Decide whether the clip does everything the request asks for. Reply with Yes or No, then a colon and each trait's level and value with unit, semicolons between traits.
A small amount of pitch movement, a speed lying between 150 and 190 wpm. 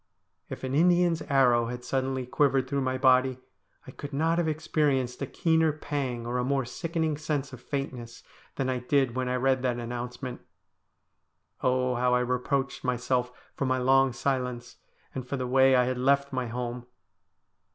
Yes: narrow, 2.1 semitones; average, 170 wpm